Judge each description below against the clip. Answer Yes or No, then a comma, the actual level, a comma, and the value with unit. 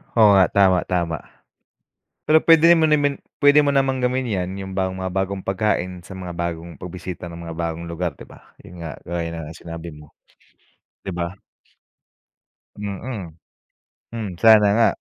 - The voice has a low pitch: Yes, very low, 95 Hz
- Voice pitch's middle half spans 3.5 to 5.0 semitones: Yes, average, 4.5 semitones